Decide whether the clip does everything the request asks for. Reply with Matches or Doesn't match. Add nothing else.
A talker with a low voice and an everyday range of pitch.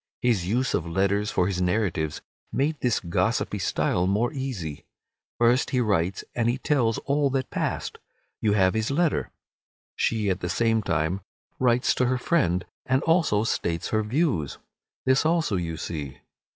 Doesn't match